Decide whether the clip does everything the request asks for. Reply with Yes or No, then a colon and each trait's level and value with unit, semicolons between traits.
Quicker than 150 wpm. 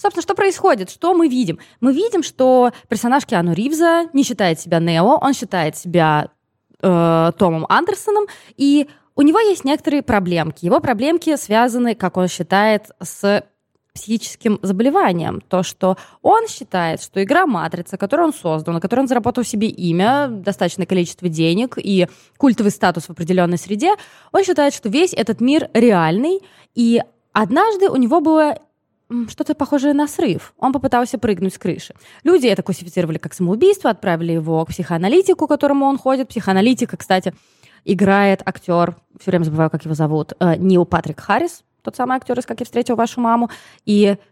Yes: fast, 160 wpm